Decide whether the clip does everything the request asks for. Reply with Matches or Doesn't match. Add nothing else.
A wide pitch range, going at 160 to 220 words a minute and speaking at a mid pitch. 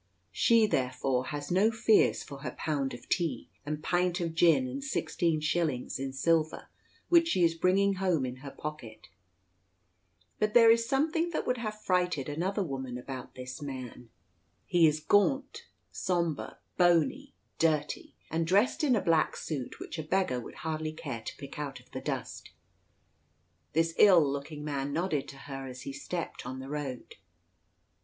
Matches